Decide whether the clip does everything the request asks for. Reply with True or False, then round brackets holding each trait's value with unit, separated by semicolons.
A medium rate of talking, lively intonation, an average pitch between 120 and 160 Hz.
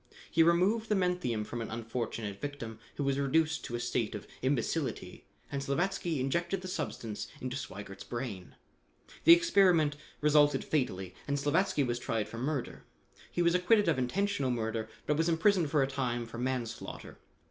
True (165 wpm; 6.2 semitones; 140 Hz)